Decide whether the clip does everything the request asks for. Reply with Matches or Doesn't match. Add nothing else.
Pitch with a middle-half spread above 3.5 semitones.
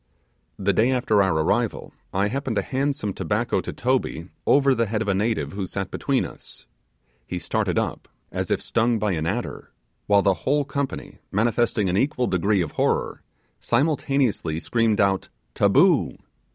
Matches